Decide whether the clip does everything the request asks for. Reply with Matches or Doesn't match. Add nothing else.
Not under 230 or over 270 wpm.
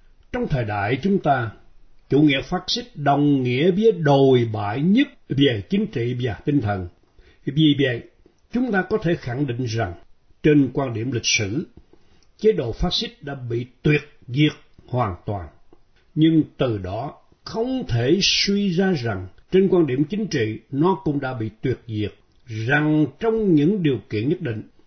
Doesn't match